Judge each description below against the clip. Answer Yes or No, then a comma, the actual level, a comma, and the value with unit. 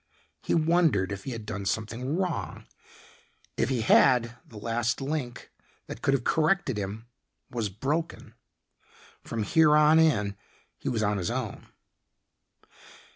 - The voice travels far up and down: Yes, wide, 6.0 semitones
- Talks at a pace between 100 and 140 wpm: Yes, slow, 135 wpm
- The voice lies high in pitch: No, low, 120 Hz